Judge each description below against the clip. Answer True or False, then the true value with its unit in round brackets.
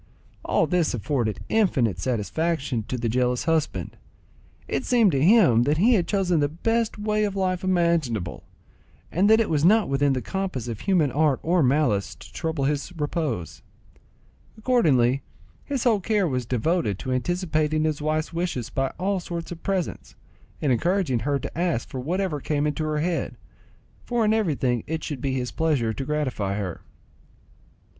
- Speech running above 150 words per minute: True (165 wpm)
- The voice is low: False (155 Hz)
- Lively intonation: True (6.1 semitones)